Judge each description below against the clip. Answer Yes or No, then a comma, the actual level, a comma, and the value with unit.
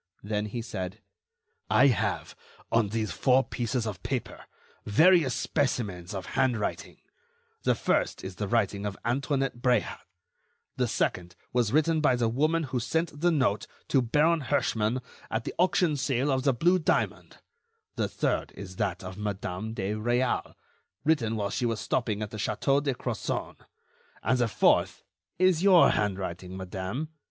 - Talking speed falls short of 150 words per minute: No, average, 155 wpm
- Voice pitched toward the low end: Yes, low, 120 Hz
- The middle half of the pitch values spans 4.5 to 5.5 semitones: Yes, average, 5.2 semitones